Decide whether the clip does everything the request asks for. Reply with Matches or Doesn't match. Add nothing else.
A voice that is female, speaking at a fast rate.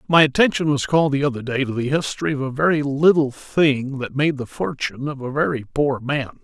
Doesn't match